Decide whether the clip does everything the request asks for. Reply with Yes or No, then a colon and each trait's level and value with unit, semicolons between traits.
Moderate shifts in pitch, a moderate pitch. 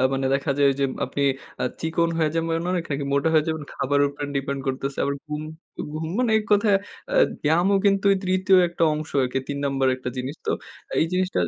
Yes: average, 3.7 semitones; medium, 150 Hz